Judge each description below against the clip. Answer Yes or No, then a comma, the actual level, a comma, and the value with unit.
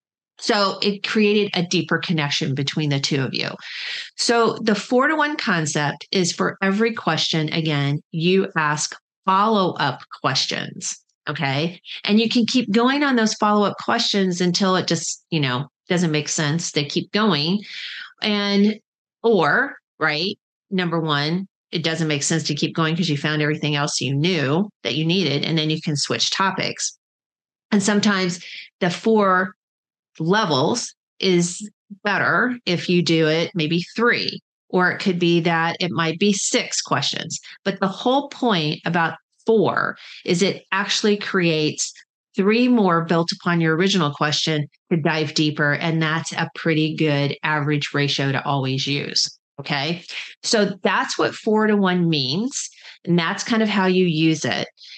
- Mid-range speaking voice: Yes, medium, 175 Hz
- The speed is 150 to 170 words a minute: Yes, average, 160 wpm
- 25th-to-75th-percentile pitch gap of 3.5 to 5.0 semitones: Yes, average, 4.5 semitones